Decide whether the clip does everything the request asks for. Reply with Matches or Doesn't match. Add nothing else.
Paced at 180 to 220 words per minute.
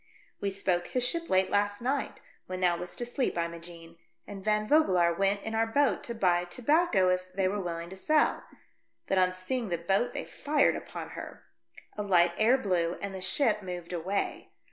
Matches